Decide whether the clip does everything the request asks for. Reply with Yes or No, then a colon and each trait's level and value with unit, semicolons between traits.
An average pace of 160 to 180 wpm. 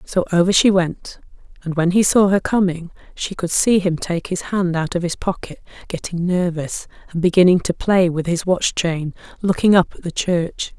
No: average, 195 wpm